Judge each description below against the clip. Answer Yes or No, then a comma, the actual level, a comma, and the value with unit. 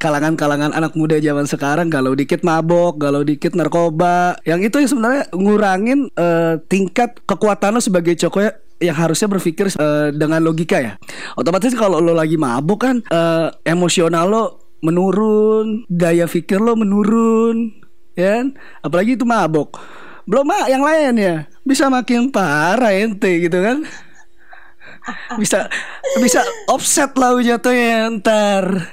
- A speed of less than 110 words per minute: No, average, 135 wpm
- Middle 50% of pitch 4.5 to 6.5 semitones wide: Yes, wide, 5.6 semitones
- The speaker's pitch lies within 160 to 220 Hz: Yes, high, 190 Hz